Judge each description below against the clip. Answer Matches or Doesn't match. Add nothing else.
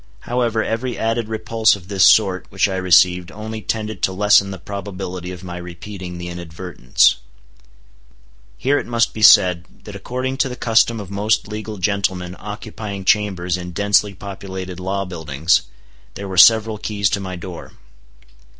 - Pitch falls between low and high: Doesn't match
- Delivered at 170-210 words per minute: Doesn't match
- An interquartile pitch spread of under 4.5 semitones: Matches